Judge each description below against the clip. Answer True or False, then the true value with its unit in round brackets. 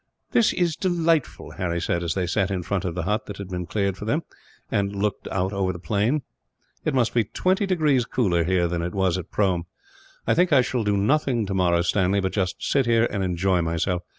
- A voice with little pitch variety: False (5.1 semitones)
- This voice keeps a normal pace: False (215 wpm)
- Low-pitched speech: True (100 Hz)